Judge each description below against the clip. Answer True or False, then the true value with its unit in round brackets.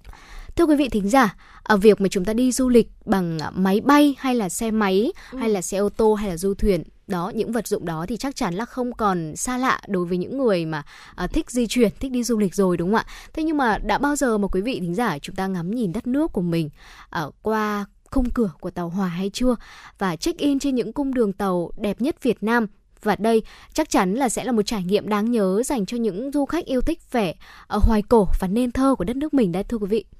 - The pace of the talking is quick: True (260 wpm)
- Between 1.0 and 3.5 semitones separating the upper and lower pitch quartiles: False (4.3 semitones)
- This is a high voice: True (220 Hz)